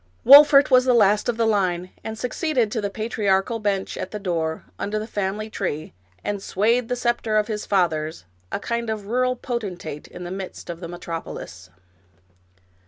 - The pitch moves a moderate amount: Yes, average, 4.3 semitones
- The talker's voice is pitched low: No, high, 210 Hz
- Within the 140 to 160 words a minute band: No, average, 185 wpm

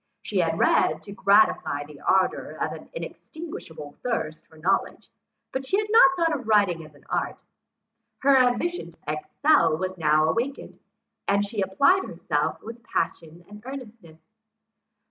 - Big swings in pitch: Yes, wide, 8.8 semitones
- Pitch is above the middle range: Yes, high, 210 Hz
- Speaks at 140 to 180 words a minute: Yes, average, 150 wpm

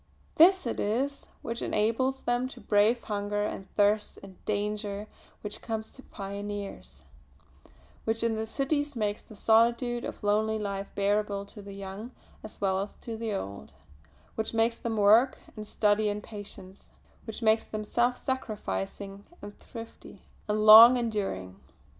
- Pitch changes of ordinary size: No, narrow, 2.2 semitones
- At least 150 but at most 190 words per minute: Yes, average, 155 wpm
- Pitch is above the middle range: Yes, high, 215 Hz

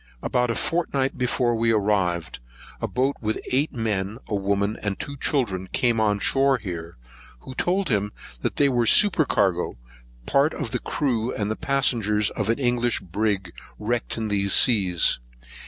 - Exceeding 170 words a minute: No, average, 155 wpm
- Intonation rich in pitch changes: No, average, 4.3 semitones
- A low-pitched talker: Yes, low, 110 Hz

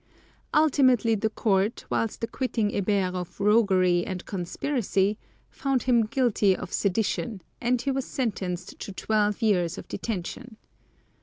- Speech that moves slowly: Yes, slow, 130 wpm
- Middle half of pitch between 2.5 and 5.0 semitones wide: Yes, average, 4.1 semitones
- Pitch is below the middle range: No, high, 210 Hz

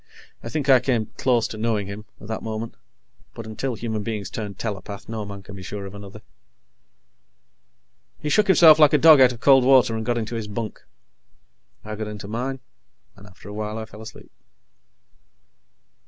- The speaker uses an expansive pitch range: No, average, 3.2 semitones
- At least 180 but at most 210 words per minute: Yes, average, 185 wpm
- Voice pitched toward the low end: Yes, low, 110 Hz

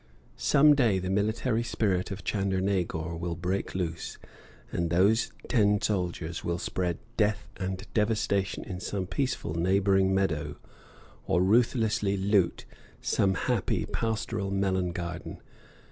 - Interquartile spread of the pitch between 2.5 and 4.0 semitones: Yes, average, 2.9 semitones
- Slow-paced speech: Yes, slow, 120 wpm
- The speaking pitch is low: Yes, very low, 95 Hz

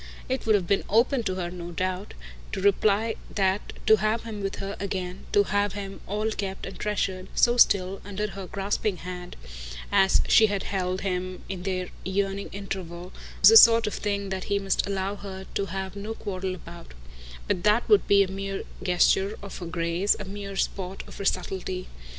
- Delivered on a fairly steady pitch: Yes, narrow, 1.7 semitones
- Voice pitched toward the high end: Yes, high, 195 Hz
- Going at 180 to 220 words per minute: Yes, average, 190 wpm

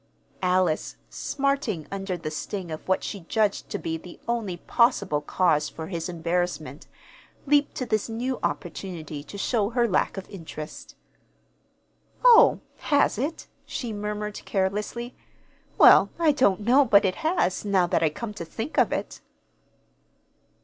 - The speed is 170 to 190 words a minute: No, average, 145 wpm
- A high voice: Yes, high, 200 Hz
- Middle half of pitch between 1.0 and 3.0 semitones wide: No, wide, 5.6 semitones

